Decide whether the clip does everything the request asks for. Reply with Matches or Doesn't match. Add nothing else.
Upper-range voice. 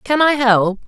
Matches